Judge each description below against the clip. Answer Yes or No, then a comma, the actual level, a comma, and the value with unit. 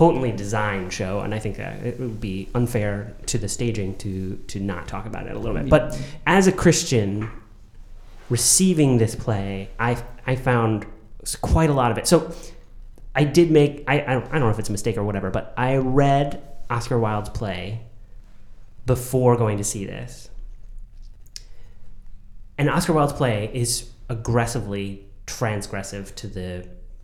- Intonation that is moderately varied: Yes, average, 4.2 semitones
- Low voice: Yes, low, 110 Hz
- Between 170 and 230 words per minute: No, average, 160 wpm